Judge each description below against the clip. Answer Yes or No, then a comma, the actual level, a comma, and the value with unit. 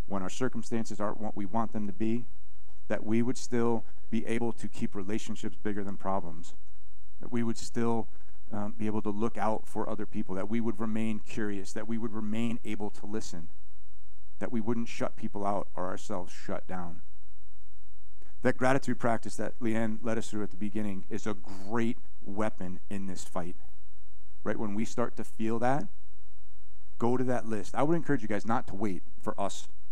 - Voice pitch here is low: Yes, low, 105 Hz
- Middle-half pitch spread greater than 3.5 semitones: No, average, 2.9 semitones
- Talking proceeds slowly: No, average, 195 wpm